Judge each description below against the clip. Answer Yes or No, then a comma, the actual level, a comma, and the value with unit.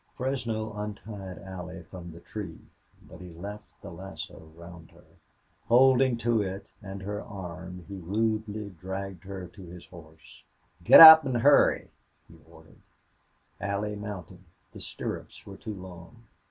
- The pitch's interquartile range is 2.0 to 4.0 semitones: Yes, average, 3.3 semitones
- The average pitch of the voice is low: Yes, low, 100 Hz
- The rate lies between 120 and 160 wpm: Yes, average, 140 wpm